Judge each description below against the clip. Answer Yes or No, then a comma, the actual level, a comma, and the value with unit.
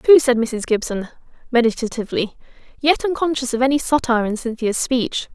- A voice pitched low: No, very high, 250 Hz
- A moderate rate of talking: Yes, average, 145 wpm